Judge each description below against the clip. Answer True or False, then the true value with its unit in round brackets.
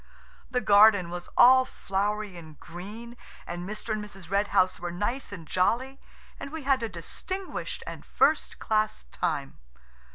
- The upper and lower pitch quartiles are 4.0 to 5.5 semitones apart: True (4.7 semitones)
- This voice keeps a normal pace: True (155 wpm)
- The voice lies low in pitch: False (210 Hz)